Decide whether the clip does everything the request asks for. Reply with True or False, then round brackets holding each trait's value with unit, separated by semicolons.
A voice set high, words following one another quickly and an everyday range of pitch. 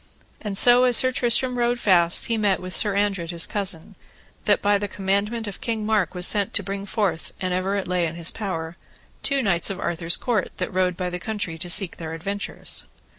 True (195 Hz; 215 wpm; 3.3 semitones)